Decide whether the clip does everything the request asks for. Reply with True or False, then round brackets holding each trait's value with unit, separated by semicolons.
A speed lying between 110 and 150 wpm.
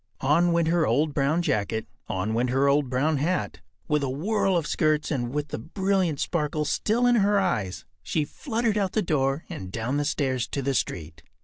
False (200 wpm)